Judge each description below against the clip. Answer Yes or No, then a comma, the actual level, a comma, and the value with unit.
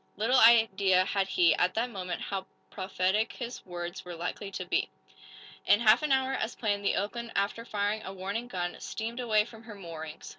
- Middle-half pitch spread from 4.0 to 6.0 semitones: No, average, 3.5 semitones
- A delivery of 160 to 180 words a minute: No, average, 190 wpm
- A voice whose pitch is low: No, high, 205 Hz